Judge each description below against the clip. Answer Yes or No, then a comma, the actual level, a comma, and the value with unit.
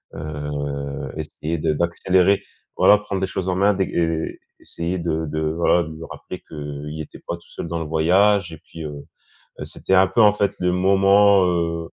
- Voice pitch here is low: Yes, very low, 85 Hz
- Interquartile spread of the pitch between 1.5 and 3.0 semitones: No, average, 3.5 semitones